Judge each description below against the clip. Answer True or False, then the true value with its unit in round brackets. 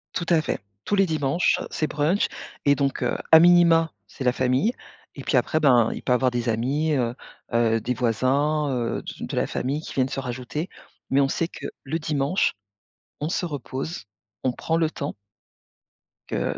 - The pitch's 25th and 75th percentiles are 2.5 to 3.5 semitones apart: False (4.1 semitones)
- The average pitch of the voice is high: False (140 Hz)